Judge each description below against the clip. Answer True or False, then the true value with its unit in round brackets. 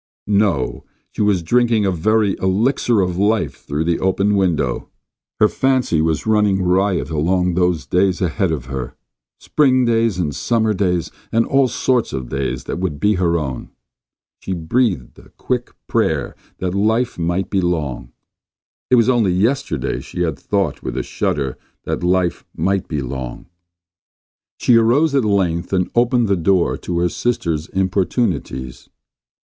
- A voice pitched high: False (95 Hz)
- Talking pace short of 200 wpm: True (155 wpm)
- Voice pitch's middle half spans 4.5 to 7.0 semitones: True (5.0 semitones)